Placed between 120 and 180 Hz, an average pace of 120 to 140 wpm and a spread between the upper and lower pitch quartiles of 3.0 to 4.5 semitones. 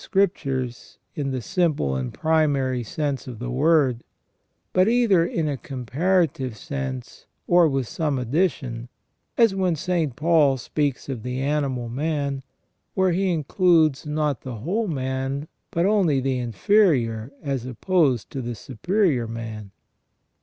No: medium, 140 Hz; slow, 135 wpm; average, 5.0 semitones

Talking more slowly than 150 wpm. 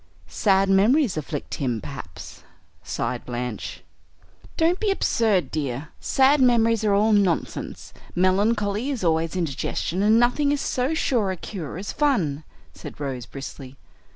Yes: slow, 135 wpm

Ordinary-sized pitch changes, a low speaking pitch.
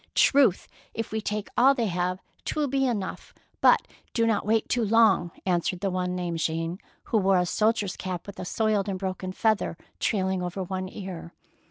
No: average, 3.4 semitones; high, 195 Hz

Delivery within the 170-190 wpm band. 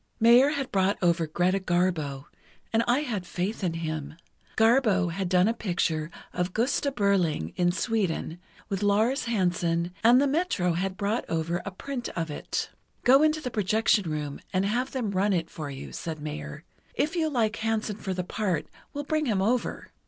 Yes: average, 180 wpm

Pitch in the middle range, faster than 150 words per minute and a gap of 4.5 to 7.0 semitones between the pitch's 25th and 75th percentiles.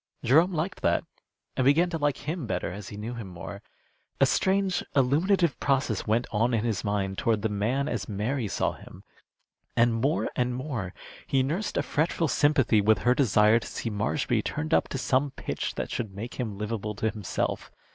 No: low, 120 Hz; average, 190 wpm; average, 5.3 semitones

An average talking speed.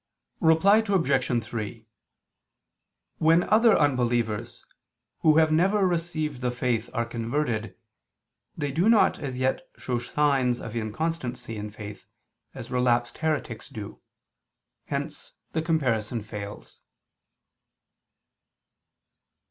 No: slow, 100 wpm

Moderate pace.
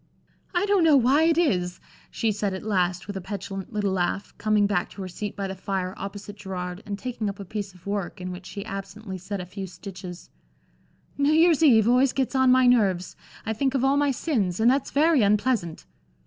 No: fast, 215 wpm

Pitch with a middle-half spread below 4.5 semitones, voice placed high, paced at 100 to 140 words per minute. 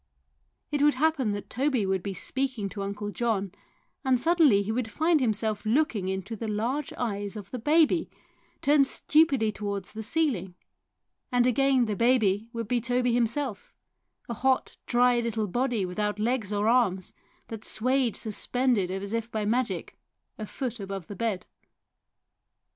No: average, 4.0 semitones; high, 230 Hz; average, 155 wpm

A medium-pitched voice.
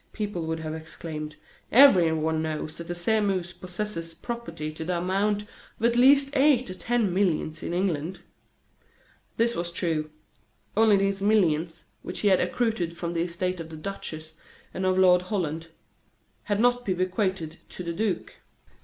Yes: medium, 180 Hz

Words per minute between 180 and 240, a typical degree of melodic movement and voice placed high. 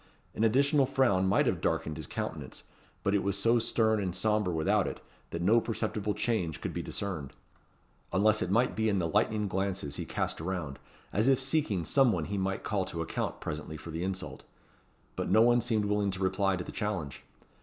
No: average, 200 wpm; average, 3.3 semitones; low, 100 Hz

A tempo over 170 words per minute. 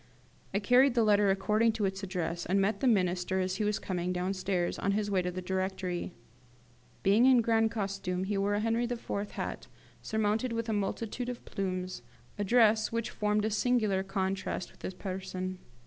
Yes: average, 185 wpm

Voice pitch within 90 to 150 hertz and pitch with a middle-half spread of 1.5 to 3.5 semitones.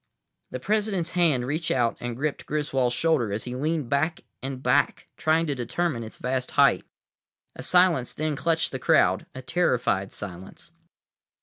No: medium, 140 Hz; average, 4.9 semitones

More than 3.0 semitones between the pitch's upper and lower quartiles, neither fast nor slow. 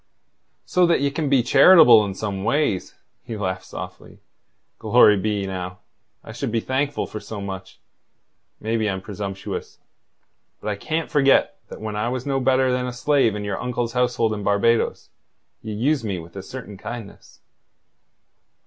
Yes: average, 4.4 semitones; average, 165 wpm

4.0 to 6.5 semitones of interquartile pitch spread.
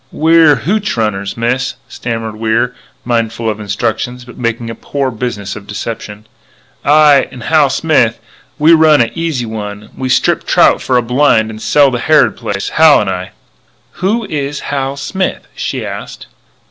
Yes: average, 4.9 semitones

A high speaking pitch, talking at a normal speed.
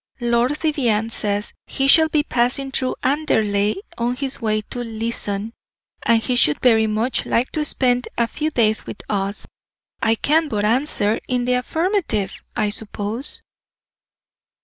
Yes: high, 235 Hz; average, 150 wpm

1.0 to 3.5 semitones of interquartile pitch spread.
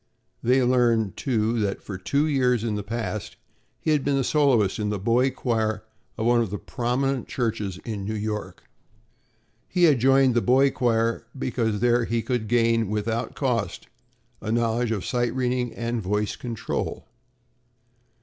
Yes: narrow, 2.6 semitones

